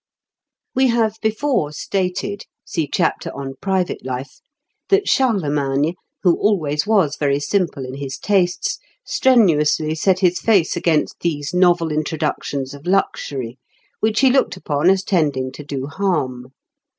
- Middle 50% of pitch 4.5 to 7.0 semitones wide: Yes, wide, 5.5 semitones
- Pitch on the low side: No, medium, 165 Hz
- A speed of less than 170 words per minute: Yes, average, 140 wpm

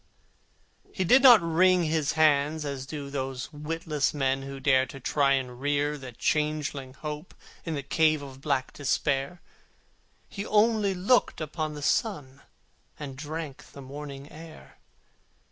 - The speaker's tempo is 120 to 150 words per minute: Yes, average, 145 wpm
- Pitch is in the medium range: Yes, medium, 150 Hz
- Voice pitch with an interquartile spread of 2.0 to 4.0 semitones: Yes, average, 2.8 semitones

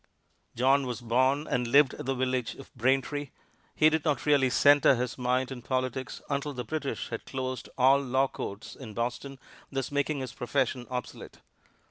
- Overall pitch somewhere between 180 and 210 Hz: No, low, 130 Hz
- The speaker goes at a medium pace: Yes, average, 170 wpm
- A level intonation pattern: Yes, narrow, 2.0 semitones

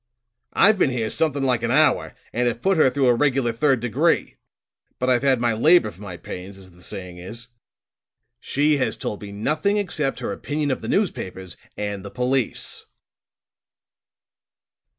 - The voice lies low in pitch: Yes, low, 125 Hz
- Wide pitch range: Yes, wide, 5.9 semitones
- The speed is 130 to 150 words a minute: No, average, 170 wpm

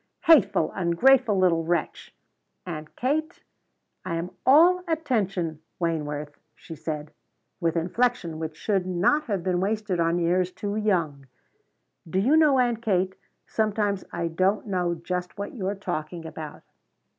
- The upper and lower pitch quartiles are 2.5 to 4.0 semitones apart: No, average, 4.5 semitones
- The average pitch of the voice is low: No, medium, 185 Hz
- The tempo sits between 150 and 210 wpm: No, slow, 135 wpm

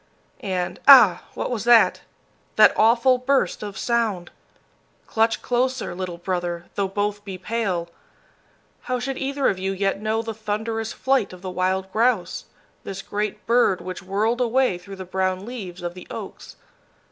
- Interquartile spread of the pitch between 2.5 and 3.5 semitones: No, average, 4.1 semitones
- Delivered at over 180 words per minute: No, average, 160 wpm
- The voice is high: Yes, high, 205 Hz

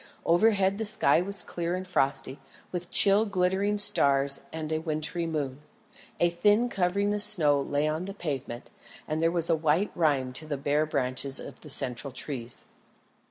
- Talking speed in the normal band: Yes, average, 170 wpm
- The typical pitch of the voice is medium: Yes, medium, 160 Hz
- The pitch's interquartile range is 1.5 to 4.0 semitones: No, average, 5.0 semitones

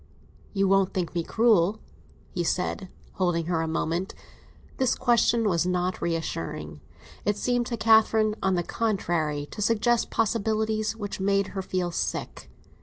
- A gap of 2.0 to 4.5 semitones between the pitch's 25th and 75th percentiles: Yes, average, 4.1 semitones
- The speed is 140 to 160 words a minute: Yes, average, 145 wpm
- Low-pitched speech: No, high, 195 Hz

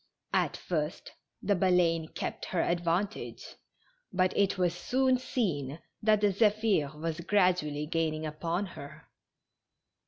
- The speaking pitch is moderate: Yes, medium, 175 Hz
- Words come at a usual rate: No, slow, 120 wpm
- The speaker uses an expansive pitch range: No, average, 4.3 semitones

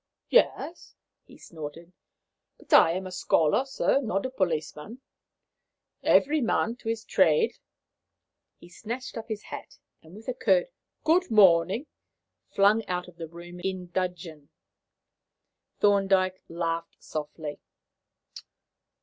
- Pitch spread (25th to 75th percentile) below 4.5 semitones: No, average, 5.2 semitones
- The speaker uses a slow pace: Yes, slow, 120 wpm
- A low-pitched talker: No, medium, 185 Hz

